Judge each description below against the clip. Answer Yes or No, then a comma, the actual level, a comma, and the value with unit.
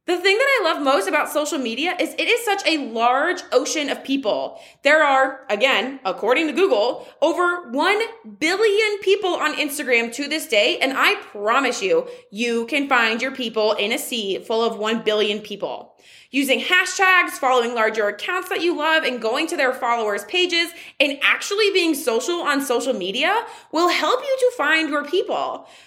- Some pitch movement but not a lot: No, wide, 7.0 semitones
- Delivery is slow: No, average, 180 wpm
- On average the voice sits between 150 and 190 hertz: No, very high, 295 Hz